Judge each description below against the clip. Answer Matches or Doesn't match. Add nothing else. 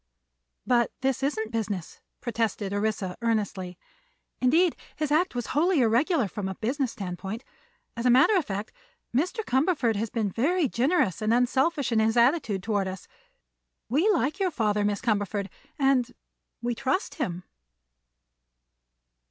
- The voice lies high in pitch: Matches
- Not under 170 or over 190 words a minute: Doesn't match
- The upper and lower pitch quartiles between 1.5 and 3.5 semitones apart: Doesn't match